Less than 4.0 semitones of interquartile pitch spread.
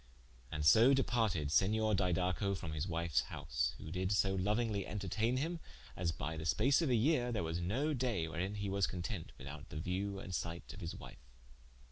No: average, 5.1 semitones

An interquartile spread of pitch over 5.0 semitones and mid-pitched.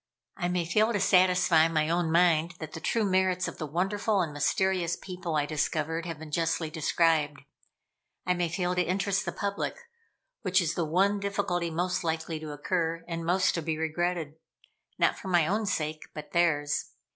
No: narrow, 2.5 semitones; medium, 170 Hz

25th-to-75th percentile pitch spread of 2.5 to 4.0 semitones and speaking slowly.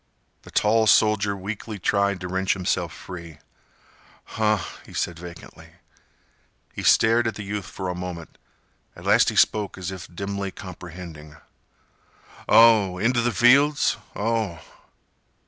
Yes: average, 3.3 semitones; slow, 130 wpm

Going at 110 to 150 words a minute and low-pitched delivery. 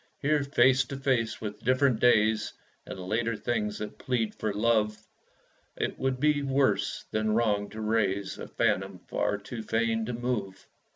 No: average, 160 wpm; low, 115 Hz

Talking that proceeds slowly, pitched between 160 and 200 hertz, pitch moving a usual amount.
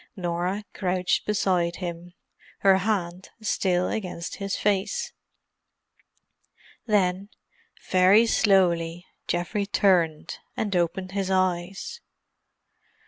No: slow, 85 wpm; medium, 185 Hz; narrow, 2.2 semitones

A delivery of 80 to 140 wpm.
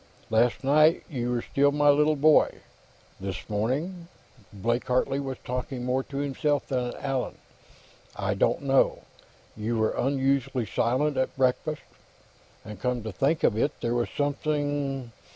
No: average, 150 wpm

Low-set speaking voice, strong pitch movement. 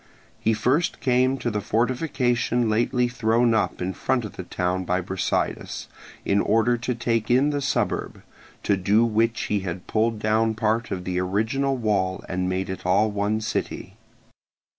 No: low, 110 Hz; average, 4.0 semitones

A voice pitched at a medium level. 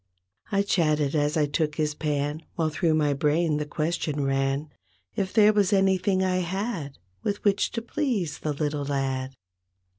Yes: medium, 155 Hz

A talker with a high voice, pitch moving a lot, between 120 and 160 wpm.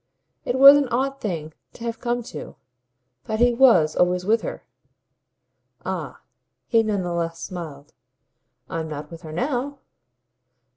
Yes: high, 215 Hz; wide, 6.7 semitones; average, 145 wpm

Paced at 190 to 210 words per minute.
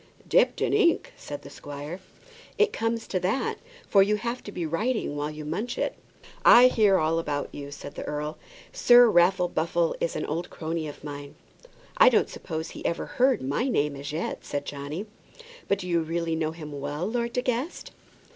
Yes: average, 195 wpm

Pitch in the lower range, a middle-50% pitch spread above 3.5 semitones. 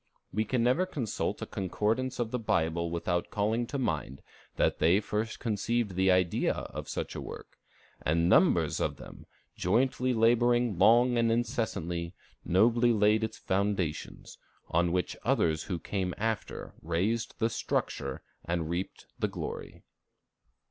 Yes: low, 105 Hz; average, 5.1 semitones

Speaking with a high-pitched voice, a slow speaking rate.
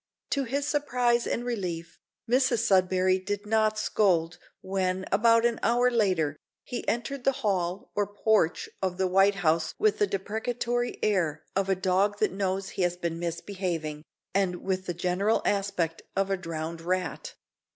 No: high, 195 Hz; average, 160 wpm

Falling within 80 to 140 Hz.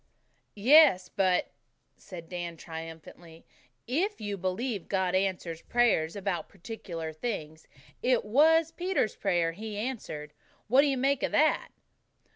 No: high, 195 Hz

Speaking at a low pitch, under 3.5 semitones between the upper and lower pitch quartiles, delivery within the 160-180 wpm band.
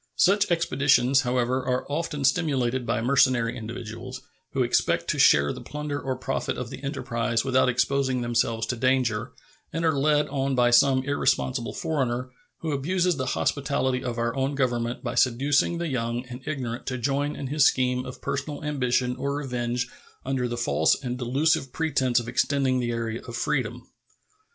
Yes: low, 130 Hz; narrow, 2.5 semitones; average, 170 wpm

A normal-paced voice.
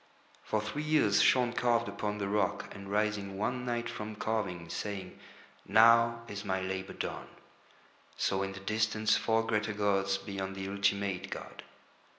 Yes: average, 155 wpm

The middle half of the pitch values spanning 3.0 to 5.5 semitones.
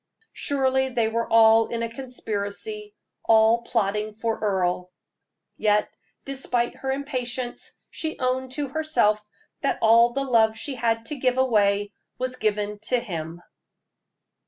Yes: average, 3.6 semitones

